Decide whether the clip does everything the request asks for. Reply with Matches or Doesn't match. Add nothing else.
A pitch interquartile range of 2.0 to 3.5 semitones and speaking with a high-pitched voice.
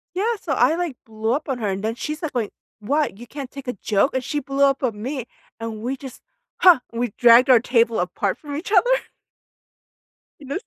Doesn't match